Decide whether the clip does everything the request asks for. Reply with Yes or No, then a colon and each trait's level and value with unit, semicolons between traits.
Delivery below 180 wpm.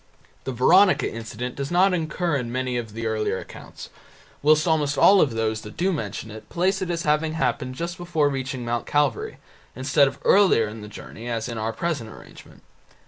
No: average, 195 wpm